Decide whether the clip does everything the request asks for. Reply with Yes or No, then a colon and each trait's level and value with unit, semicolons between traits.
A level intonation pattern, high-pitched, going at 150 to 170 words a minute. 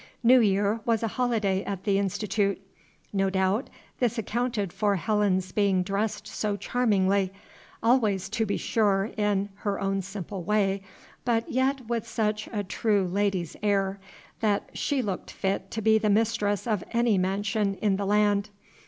Yes: narrow, 2.2 semitones; high, 205 Hz; average, 155 wpm